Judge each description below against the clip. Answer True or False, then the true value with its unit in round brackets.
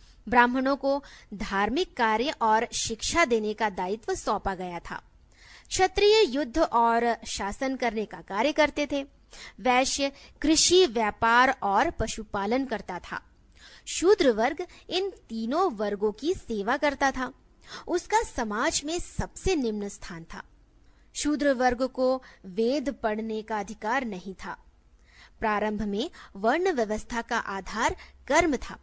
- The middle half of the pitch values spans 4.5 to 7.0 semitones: True (5.3 semitones)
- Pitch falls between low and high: False (245 Hz)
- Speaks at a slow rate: False (125 wpm)